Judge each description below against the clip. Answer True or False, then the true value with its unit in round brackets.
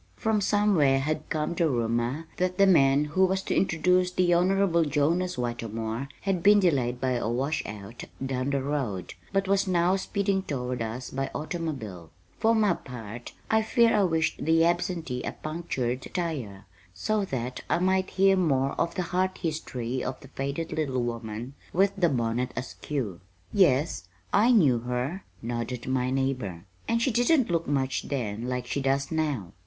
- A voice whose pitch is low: False (145 Hz)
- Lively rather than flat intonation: True (6.7 semitones)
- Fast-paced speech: False (165 wpm)